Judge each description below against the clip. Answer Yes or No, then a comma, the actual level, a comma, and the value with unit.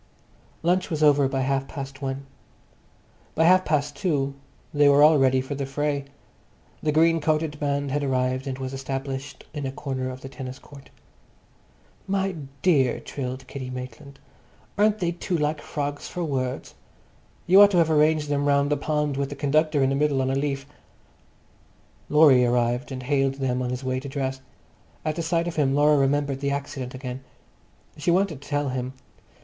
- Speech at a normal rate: Yes, average, 180 wpm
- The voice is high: No, medium, 140 Hz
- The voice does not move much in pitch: Yes, narrow, 2.2 semitones